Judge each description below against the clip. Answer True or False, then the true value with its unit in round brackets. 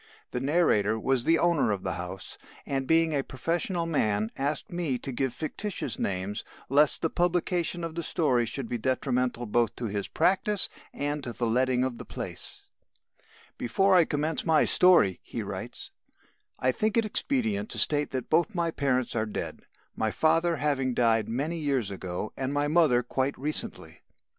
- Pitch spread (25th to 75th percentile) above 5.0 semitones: True (5.6 semitones)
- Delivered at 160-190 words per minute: True (170 wpm)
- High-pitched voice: False (140 Hz)